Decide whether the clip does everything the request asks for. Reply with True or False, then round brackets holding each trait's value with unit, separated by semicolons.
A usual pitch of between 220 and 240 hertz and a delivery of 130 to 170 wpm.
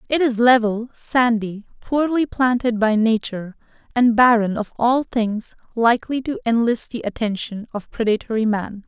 True (230 Hz; 140 wpm)